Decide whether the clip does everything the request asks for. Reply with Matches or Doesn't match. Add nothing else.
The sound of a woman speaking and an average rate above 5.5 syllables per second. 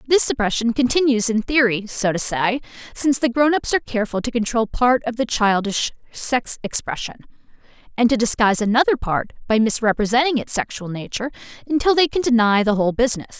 Matches